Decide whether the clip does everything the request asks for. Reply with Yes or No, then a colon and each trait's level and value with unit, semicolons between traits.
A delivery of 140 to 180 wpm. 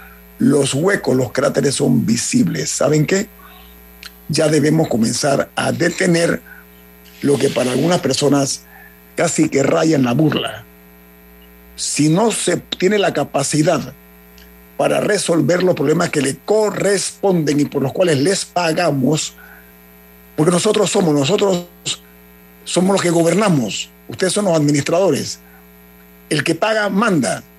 No: average, 130 wpm